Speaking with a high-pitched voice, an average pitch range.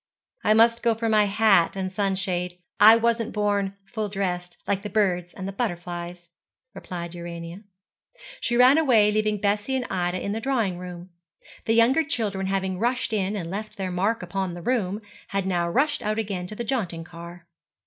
Yes: high, 200 Hz; average, 3.7 semitones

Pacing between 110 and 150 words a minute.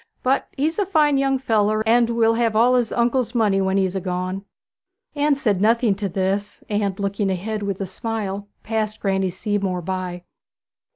No: average, 170 wpm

